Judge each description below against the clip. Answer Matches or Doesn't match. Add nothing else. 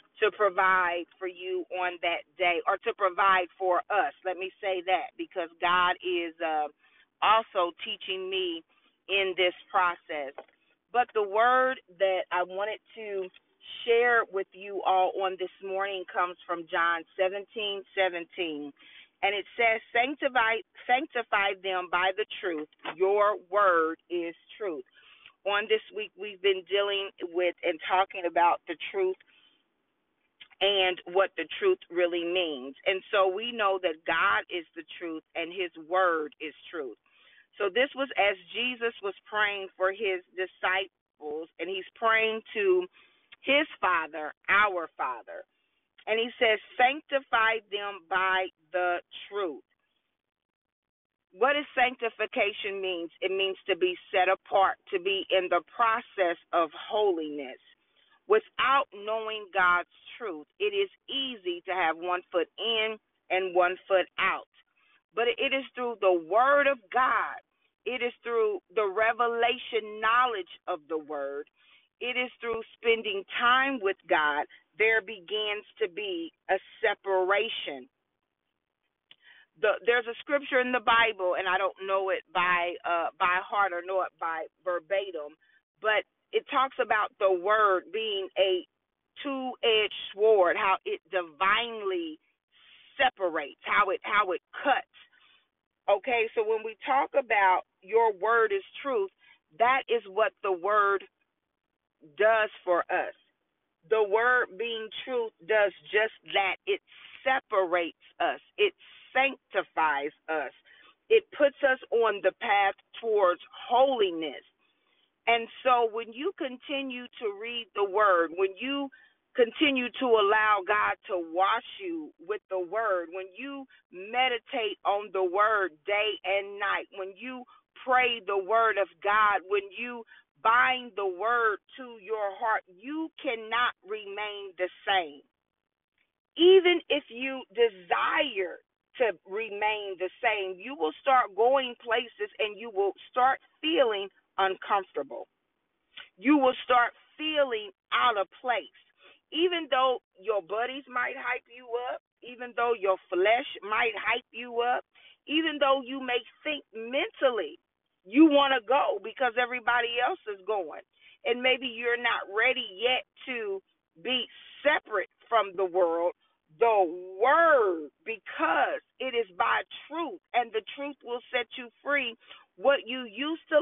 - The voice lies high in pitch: Matches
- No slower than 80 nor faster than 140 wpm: Matches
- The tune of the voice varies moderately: Doesn't match